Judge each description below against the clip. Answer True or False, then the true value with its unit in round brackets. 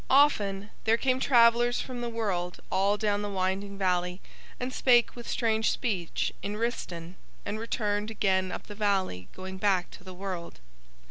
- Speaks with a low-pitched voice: False (205 Hz)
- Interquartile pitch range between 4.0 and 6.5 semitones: False (3.6 semitones)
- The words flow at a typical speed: True (160 wpm)